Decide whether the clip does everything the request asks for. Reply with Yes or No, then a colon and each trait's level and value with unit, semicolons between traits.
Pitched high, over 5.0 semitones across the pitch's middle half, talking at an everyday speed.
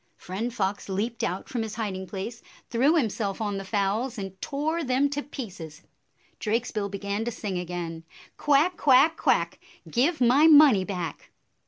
Yes: high, 220 Hz; wide, 5.6 semitones; average, 165 wpm